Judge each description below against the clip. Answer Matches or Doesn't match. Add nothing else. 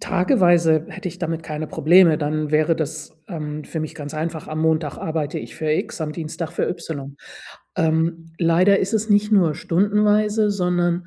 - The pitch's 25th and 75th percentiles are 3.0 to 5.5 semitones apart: Doesn't match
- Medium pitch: Matches